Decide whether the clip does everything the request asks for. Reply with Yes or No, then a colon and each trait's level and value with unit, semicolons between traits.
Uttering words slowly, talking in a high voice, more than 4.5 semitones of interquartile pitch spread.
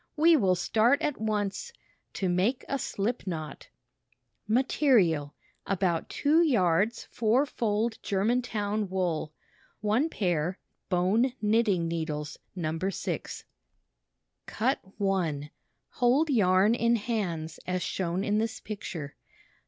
Yes: slow, 115 wpm; high, 205 Hz; average, 4.9 semitones